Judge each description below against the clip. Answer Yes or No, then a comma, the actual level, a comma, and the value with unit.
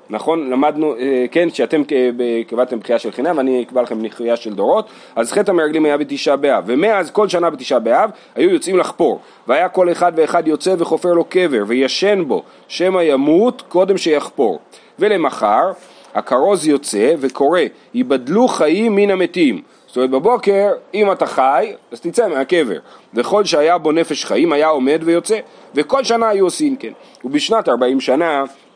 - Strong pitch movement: Yes, wide, 7.0 semitones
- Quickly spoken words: Yes, fast, 155 wpm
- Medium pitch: Yes, medium, 170 Hz